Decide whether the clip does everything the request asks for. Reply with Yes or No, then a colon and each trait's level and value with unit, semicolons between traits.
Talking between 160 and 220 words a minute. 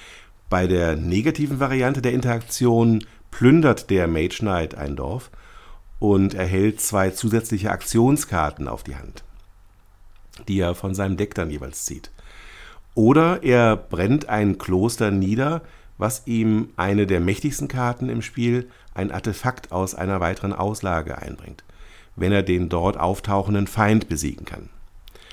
No: average, 135 wpm